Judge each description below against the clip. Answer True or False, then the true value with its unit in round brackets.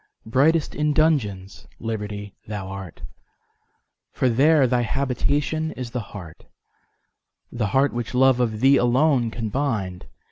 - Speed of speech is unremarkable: False (115 wpm)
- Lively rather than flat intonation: False (4.9 semitones)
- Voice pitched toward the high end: False (120 Hz)